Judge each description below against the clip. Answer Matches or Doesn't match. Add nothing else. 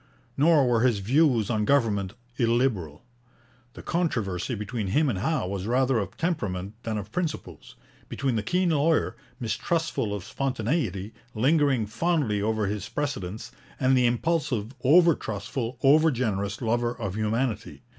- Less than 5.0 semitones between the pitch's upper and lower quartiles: Doesn't match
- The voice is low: Matches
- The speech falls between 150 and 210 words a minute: Doesn't match